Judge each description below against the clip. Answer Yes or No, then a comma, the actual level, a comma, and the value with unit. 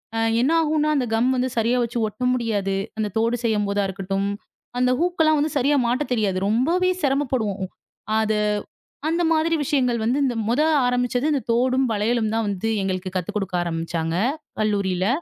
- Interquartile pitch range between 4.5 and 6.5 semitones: Yes, average, 4.8 semitones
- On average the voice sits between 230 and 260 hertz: Yes, high, 235 Hz